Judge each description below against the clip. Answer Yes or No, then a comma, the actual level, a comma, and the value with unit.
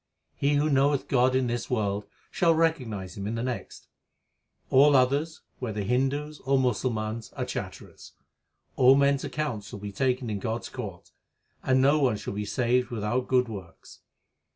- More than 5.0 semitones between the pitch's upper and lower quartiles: No, average, 4.3 semitones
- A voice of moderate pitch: No, low, 125 Hz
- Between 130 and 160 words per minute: No, average, 170 wpm